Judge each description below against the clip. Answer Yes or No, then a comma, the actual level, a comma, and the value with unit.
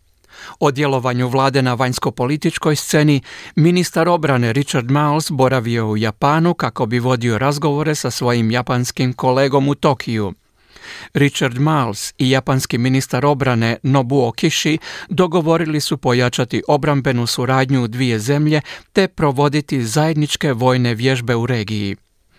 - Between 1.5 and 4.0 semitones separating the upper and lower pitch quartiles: Yes, average, 3.2 semitones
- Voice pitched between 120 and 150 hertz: Yes, low, 135 Hz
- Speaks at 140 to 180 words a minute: No, average, 125 wpm